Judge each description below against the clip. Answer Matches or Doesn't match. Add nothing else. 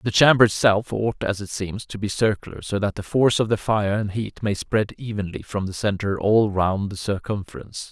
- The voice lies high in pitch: Doesn't match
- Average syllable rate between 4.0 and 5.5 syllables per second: Matches